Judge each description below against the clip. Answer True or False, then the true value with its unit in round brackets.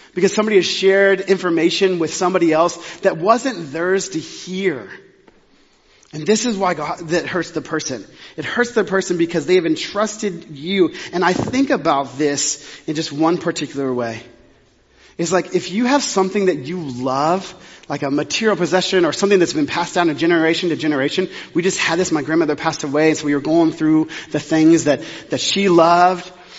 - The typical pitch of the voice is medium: True (170 Hz)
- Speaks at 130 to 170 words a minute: False (190 wpm)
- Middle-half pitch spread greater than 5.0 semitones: False (3.4 semitones)